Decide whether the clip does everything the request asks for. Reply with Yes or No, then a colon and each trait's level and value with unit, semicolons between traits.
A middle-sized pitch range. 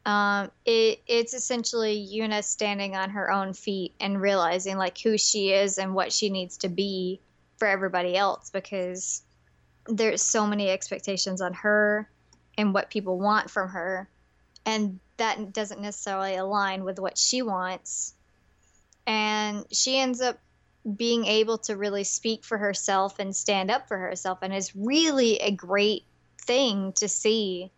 No: narrow, 2.1 semitones